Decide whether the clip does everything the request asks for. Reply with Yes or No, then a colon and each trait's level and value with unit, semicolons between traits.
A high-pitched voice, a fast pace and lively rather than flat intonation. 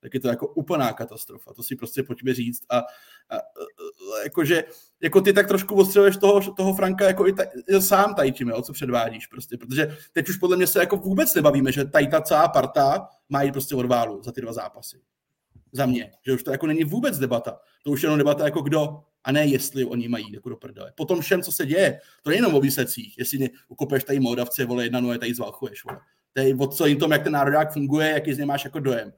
No: medium, 140 Hz; fast, 230 wpm; wide, 6.1 semitones